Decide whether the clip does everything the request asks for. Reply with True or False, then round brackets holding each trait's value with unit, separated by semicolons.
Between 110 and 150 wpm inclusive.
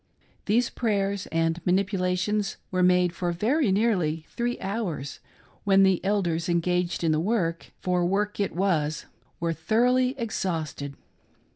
True (140 wpm)